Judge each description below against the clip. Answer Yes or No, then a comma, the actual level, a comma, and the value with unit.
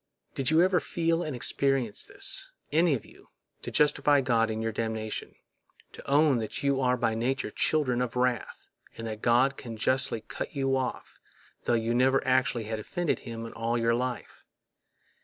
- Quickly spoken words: No, average, 170 wpm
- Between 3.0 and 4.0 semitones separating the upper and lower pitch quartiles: Yes, average, 3.3 semitones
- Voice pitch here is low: Yes, low, 125 Hz